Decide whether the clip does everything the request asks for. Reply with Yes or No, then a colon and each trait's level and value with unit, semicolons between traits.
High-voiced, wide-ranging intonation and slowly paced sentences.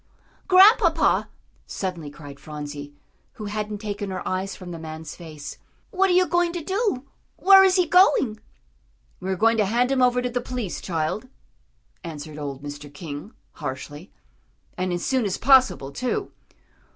No: high, 205 Hz; wide, 8.8 semitones; average, 160 wpm